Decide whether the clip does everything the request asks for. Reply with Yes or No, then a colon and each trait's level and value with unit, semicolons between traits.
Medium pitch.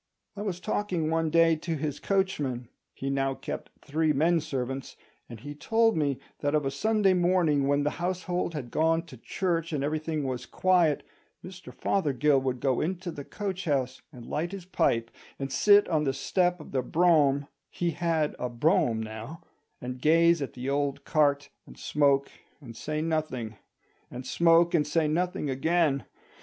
Yes: medium, 155 Hz